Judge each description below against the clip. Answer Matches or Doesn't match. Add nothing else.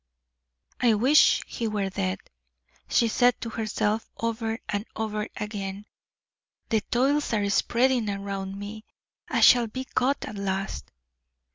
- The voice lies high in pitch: Matches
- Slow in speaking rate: Matches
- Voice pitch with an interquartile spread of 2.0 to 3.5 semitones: Matches